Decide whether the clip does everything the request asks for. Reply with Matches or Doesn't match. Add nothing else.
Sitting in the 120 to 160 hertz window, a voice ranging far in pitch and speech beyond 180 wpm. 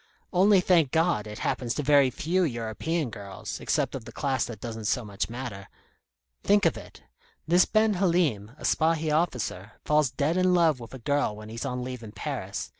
Matches